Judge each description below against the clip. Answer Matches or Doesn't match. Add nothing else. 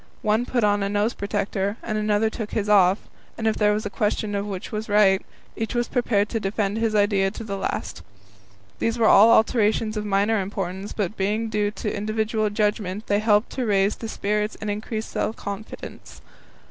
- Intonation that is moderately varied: Doesn't match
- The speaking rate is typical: Matches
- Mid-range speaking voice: Doesn't match